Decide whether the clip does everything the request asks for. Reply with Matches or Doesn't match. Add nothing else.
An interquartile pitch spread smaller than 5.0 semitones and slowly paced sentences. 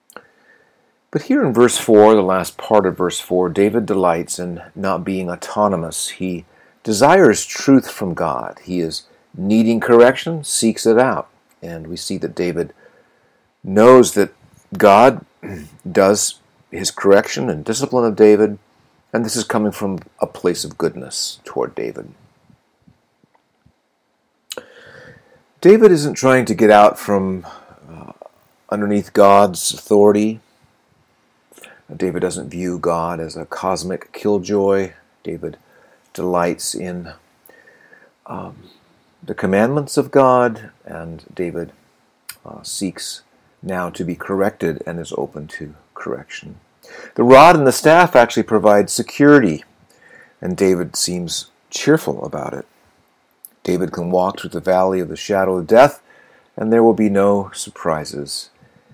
Matches